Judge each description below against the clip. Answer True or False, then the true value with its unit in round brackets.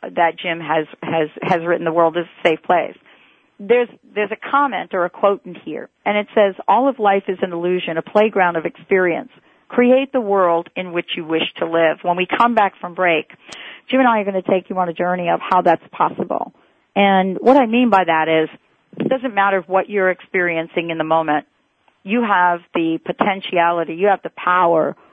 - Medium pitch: True (180 Hz)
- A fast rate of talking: True (210 wpm)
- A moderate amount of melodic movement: True (3.3 semitones)